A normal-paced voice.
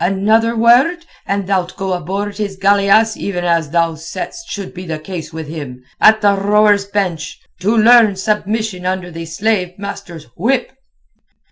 Yes: average, 150 wpm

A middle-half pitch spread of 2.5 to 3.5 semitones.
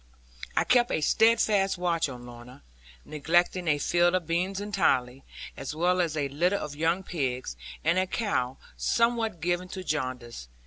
No: average, 5.0 semitones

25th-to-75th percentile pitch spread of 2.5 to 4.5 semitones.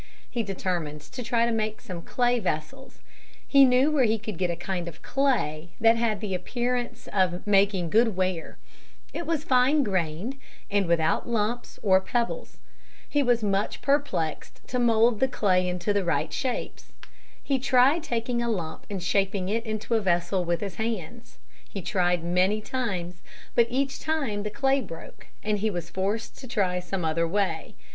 No: average, 5.1 semitones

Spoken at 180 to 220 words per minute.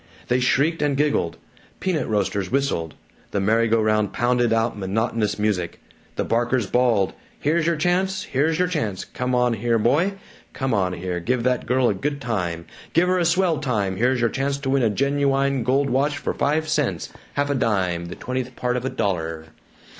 Yes: average, 190 wpm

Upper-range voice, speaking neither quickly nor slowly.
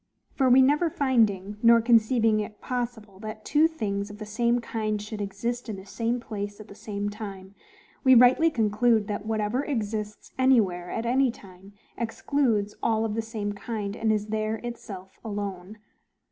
Yes: high, 220 Hz; average, 170 wpm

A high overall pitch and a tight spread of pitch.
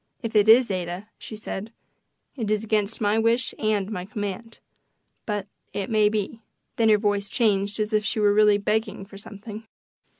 Yes: high, 210 Hz; narrow, 1.4 semitones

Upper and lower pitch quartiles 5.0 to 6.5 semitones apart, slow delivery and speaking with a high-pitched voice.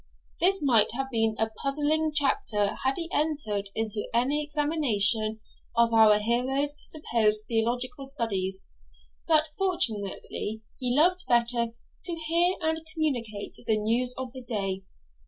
Yes: wide, 5.4 semitones; slow, 130 wpm; high, 245 Hz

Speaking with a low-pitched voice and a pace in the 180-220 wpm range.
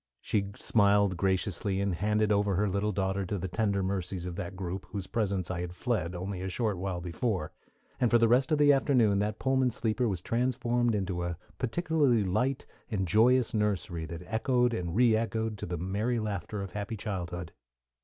Yes: low, 100 Hz; average, 185 wpm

